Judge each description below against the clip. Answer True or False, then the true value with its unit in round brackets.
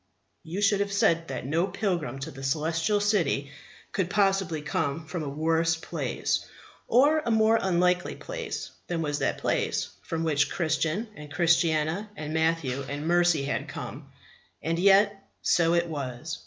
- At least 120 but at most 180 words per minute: True (160 wpm)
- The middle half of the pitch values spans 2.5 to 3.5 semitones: False (4.0 semitones)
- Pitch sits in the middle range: True (165 Hz)